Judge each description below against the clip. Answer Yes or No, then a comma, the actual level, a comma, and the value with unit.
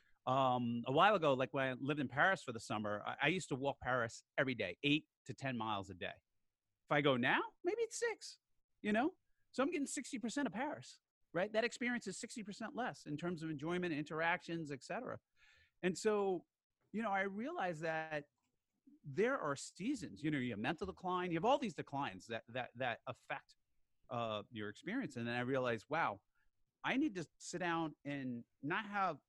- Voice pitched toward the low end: No, medium, 160 Hz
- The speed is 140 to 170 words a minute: No, average, 195 wpm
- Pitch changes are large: Yes, wide, 8.7 semitones